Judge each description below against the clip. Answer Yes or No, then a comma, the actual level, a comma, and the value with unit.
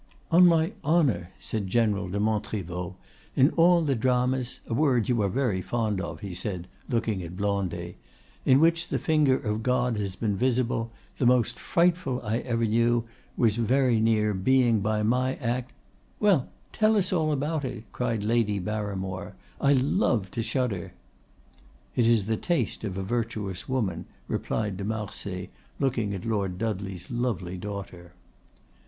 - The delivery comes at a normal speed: Yes, average, 150 wpm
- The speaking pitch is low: Yes, low, 115 Hz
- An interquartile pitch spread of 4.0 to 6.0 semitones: Yes, average, 4.4 semitones